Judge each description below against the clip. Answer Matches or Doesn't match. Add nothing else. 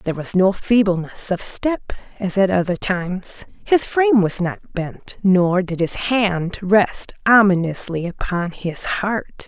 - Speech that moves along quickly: Doesn't match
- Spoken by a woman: Matches